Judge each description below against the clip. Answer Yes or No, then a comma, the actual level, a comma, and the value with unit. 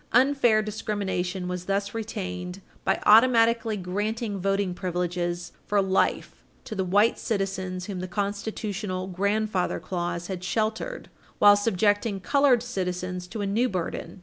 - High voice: Yes, high, 200 Hz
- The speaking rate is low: Yes, slow, 130 wpm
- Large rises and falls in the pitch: No, average, 3.1 semitones